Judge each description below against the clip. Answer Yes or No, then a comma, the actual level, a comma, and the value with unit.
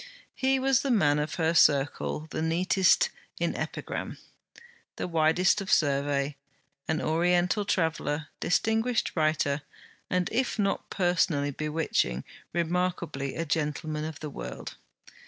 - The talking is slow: Yes, slow, 125 wpm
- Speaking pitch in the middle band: Yes, medium, 160 Hz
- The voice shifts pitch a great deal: No, average, 3.4 semitones